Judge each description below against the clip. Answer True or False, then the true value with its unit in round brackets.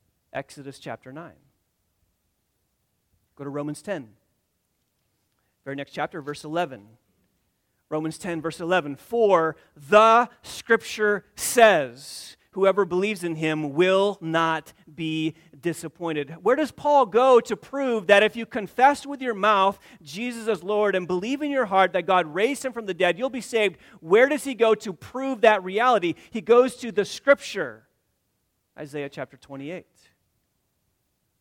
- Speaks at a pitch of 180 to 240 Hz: True (185 Hz)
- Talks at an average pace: True (145 wpm)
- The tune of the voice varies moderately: False (7.7 semitones)